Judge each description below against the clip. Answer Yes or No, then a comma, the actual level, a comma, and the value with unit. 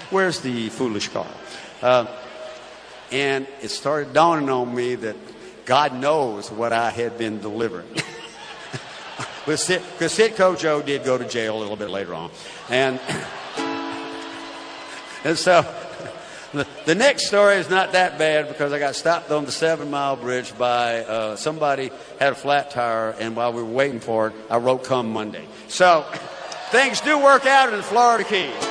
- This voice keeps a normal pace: Yes, average, 165 wpm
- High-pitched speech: No, low, 135 Hz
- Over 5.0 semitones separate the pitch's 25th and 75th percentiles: Yes, wide, 5.6 semitones